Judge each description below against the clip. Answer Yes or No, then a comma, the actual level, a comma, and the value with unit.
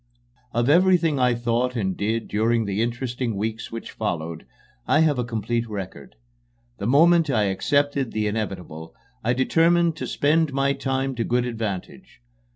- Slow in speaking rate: No, average, 155 wpm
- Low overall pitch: Yes, low, 120 Hz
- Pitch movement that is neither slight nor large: Yes, average, 4.5 semitones